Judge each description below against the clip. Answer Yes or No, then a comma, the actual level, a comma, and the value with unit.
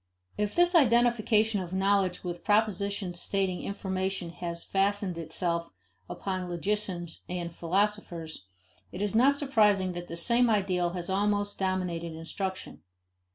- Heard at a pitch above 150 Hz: Yes, high, 190 Hz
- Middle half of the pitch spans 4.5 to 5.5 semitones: No, average, 3.0 semitones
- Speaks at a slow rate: Yes, slow, 125 wpm